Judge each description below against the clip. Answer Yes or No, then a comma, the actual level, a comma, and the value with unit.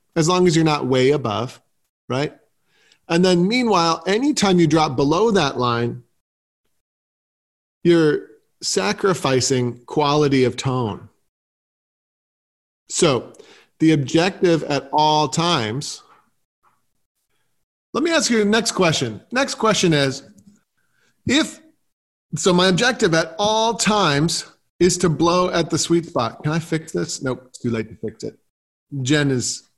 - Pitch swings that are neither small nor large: No, wide, 6.4 semitones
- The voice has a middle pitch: Yes, medium, 160 Hz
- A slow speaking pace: Yes, slow, 130 wpm